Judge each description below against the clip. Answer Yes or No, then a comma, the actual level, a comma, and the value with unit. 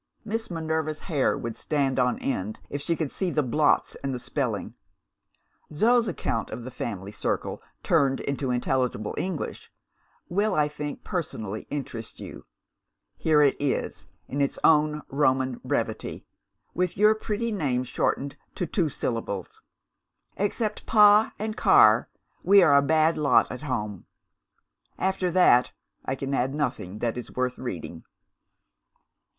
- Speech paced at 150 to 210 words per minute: No, average, 140 wpm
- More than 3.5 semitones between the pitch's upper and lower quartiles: Yes, wide, 5.6 semitones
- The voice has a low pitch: No, medium, 145 Hz